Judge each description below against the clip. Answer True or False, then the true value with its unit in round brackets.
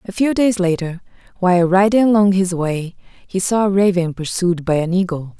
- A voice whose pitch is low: False (185 Hz)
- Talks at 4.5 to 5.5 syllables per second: True (5.1 syllables/s)